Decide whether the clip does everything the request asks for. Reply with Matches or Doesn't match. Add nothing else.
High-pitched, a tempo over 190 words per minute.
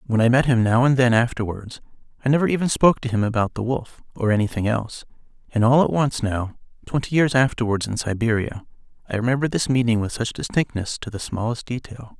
Doesn't match